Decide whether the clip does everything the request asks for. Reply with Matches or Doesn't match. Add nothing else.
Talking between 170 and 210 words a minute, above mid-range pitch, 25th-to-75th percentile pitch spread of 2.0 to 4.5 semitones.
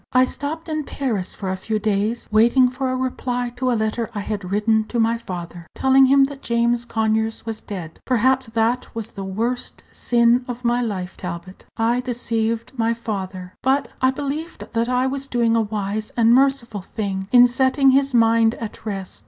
Matches